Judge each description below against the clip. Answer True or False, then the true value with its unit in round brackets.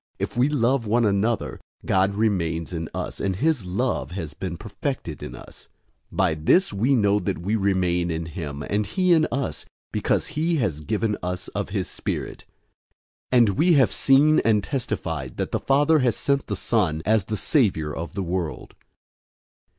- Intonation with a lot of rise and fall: True (6.8 semitones)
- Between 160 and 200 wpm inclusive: True (175 wpm)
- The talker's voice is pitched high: False (105 Hz)